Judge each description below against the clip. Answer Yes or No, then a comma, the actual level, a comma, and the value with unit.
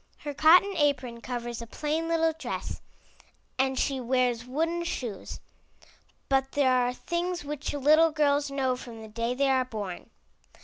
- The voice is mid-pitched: No, very high, 270 Hz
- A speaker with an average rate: Yes, average, 150 wpm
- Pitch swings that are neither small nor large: Yes, average, 3.7 semitones